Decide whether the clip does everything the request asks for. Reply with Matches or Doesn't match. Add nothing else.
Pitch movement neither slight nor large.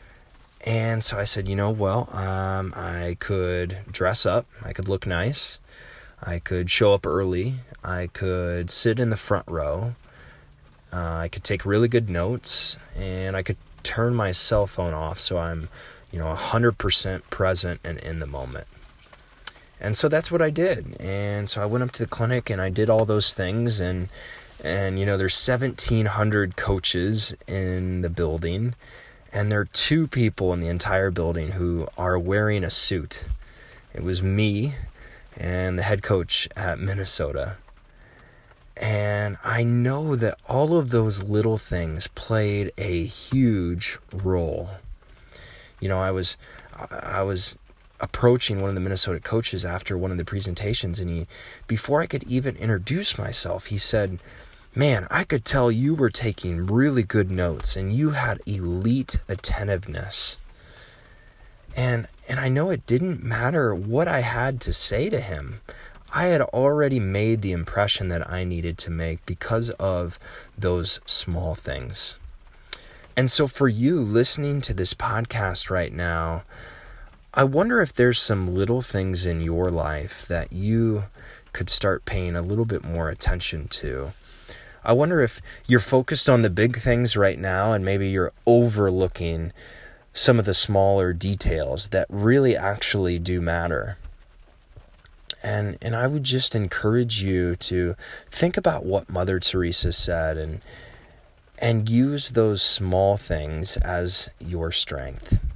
Matches